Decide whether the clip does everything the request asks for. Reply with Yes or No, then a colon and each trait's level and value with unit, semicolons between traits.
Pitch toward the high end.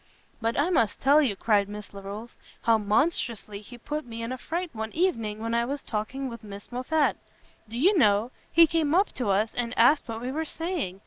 Yes: high, 235 Hz